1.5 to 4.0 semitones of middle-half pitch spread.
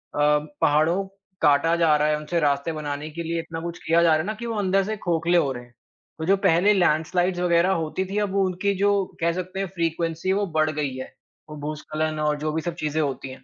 Yes: average, 3.0 semitones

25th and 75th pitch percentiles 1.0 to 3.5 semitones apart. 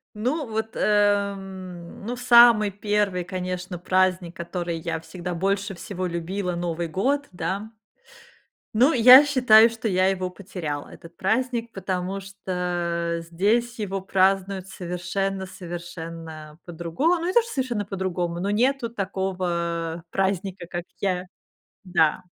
Yes: average, 3.1 semitones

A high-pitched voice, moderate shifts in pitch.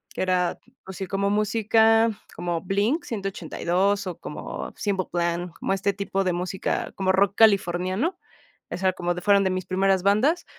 No: high, 195 Hz; narrow, 1.9 semitones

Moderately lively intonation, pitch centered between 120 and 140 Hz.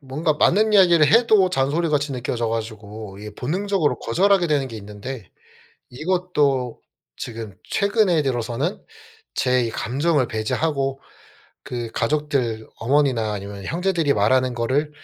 No: wide, 6.3 semitones; low, 135 Hz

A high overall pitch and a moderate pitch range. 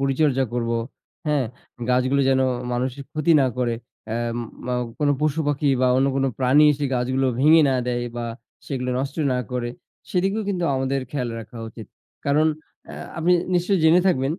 No: low, 135 Hz; average, 3.3 semitones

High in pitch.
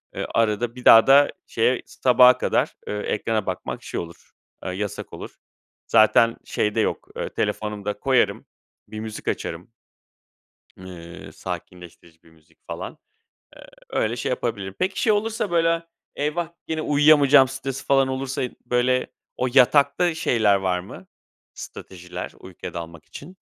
No: low, 115 Hz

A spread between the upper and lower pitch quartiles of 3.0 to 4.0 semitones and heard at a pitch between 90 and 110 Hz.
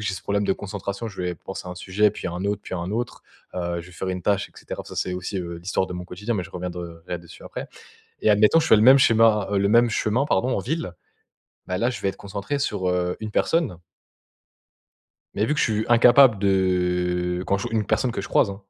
Yes: average, 3.3 semitones; low, 100 Hz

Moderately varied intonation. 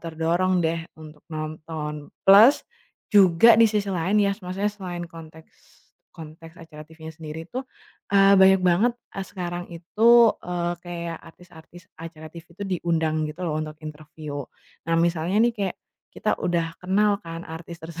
Yes: average, 3.1 semitones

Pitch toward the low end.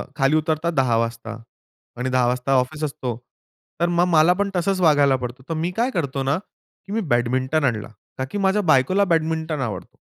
No: medium, 145 Hz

